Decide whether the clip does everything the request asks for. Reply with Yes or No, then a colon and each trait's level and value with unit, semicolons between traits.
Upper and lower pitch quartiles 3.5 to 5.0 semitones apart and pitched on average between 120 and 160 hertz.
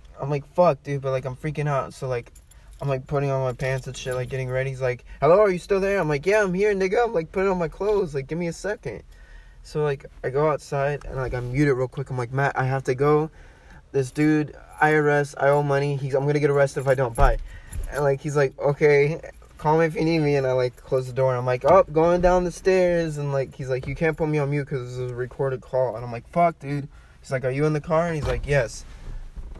No: average, 3.1 semitones; medium, 140 Hz